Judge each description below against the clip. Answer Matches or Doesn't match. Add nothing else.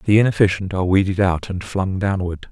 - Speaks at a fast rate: Doesn't match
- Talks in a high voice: Doesn't match